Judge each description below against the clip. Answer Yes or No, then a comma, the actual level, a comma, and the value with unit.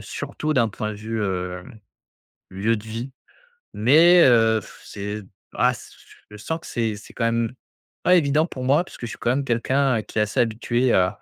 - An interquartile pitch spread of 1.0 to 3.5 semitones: No, average, 4.1 semitones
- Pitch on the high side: No, low, 115 Hz